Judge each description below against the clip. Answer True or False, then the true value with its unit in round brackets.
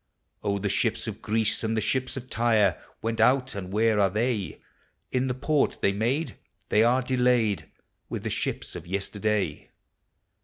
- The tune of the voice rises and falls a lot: False (3.7 semitones)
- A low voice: True (110 Hz)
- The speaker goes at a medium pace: True (165 wpm)